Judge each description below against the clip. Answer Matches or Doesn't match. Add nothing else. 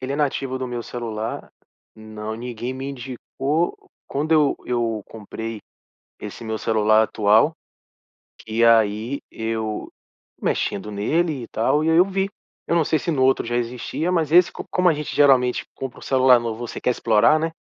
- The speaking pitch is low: Matches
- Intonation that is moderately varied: Matches